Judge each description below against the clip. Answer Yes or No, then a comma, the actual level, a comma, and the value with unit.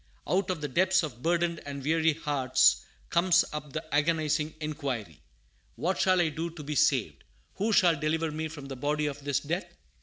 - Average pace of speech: Yes, average, 185 wpm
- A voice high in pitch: No, medium, 155 Hz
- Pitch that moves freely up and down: No, average, 2.8 semitones